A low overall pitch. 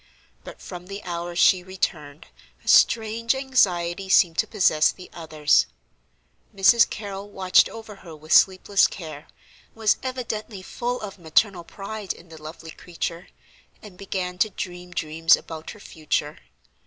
No: medium, 185 Hz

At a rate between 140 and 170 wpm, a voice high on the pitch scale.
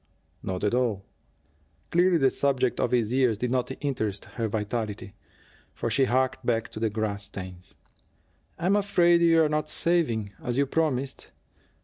No: average, 150 wpm; low, 125 Hz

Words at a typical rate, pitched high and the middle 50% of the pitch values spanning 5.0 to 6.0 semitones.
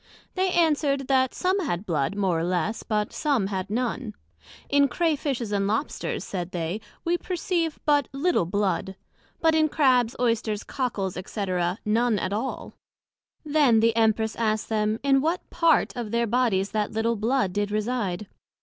Yes: average, 160 wpm; high, 230 Hz; wide, 5.4 semitones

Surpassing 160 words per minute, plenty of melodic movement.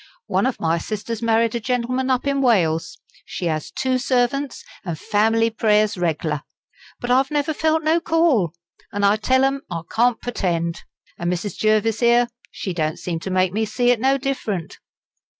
Yes: average, 175 wpm; wide, 5.7 semitones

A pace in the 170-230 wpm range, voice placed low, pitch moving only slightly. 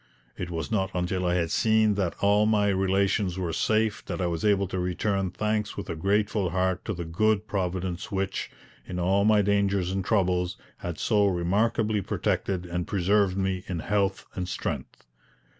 Yes: average, 175 wpm; very low, 95 Hz; narrow, 2.3 semitones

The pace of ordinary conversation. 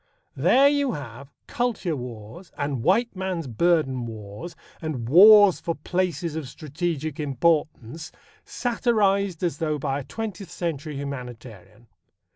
No: slow, 120 wpm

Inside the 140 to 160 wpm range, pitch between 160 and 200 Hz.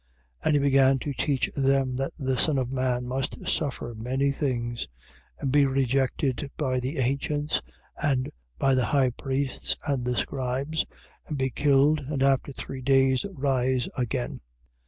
No: average, 155 wpm; low, 135 Hz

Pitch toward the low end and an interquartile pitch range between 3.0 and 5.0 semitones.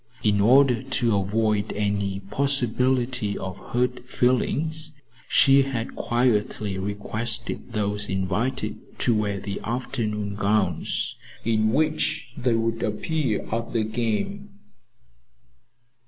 Yes: low, 115 Hz; average, 3.8 semitones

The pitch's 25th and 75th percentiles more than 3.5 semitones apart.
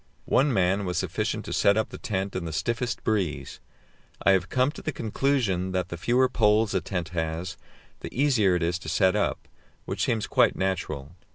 Yes: average, 4.2 semitones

